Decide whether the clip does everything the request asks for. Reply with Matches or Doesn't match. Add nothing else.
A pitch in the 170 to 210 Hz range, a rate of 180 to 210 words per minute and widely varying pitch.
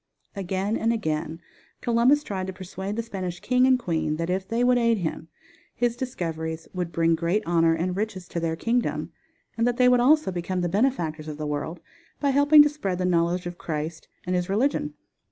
Matches